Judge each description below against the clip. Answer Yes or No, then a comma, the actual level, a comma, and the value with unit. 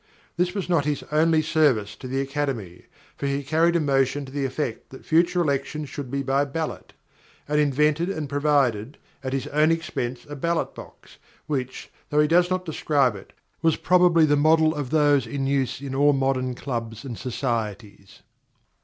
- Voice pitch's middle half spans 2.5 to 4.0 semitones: Yes, average, 3.0 semitones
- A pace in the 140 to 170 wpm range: No, average, 180 wpm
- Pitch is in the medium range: Yes, medium, 145 Hz